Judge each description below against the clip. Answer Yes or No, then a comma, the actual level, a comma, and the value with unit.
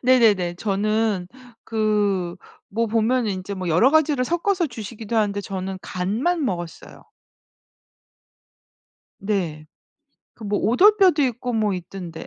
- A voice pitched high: Yes, high, 215 Hz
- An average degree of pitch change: Yes, average, 4.7 semitones